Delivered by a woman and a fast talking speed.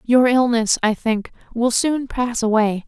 No: female; average, 165 wpm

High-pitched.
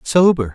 No: medium, 140 Hz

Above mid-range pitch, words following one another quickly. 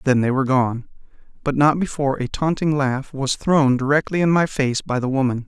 No: medium, 140 Hz; fast, 210 wpm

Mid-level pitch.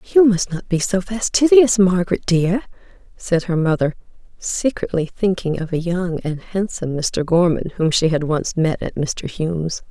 Yes: medium, 180 Hz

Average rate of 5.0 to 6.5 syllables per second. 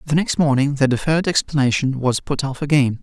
Yes: 6.0 syllables/s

